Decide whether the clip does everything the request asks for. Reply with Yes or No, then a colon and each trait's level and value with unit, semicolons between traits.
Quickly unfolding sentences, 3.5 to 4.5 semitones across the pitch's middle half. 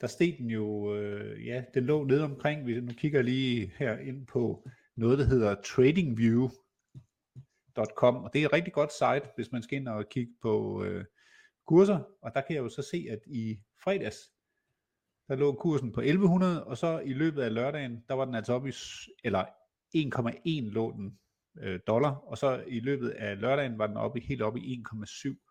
No: average, 200 wpm; average, 3.9 semitones